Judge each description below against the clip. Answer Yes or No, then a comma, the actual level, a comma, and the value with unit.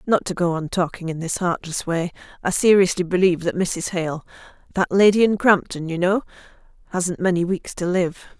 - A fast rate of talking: No, average, 170 wpm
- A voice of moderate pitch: Yes, medium, 180 Hz